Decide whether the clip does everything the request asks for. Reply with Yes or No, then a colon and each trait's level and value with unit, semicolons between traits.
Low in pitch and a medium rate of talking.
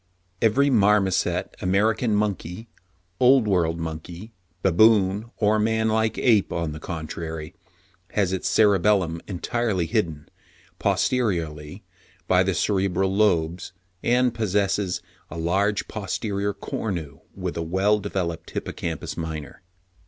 No: very low, 95 Hz; slow, 110 wpm